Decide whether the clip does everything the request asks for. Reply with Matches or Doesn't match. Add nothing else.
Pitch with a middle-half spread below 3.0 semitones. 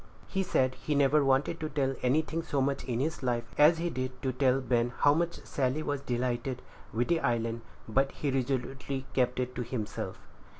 Matches